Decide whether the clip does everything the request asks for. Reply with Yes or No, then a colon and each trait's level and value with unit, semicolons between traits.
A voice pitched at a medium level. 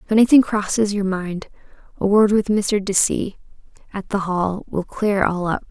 No: high, 200 Hz